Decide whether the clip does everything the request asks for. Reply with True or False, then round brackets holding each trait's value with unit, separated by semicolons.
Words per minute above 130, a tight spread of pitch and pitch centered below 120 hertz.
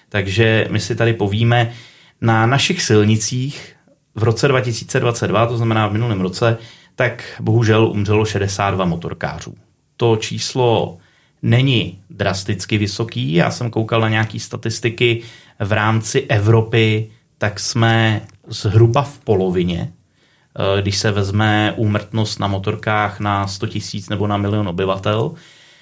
False (125 wpm; 2.1 semitones; 110 Hz)